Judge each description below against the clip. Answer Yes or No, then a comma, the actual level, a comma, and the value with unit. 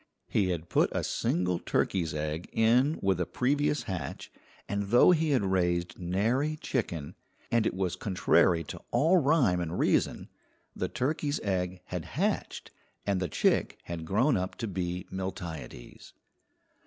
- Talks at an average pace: Yes, average, 150 wpm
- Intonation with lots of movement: Yes, wide, 6.0 semitones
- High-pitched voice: No, very low, 95 Hz